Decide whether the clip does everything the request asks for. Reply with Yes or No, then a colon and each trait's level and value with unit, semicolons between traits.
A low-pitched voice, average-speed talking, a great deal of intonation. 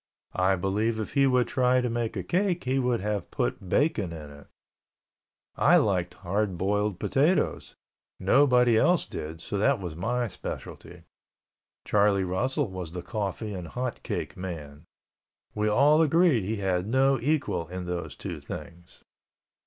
Yes: low, 105 Hz; average, 155 wpm; wide, 5.8 semitones